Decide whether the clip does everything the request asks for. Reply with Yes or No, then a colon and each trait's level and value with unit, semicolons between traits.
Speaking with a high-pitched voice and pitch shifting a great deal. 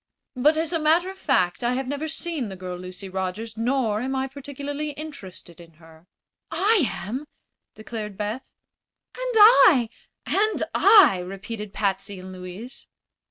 Yes: high, 240 Hz; wide, 7.9 semitones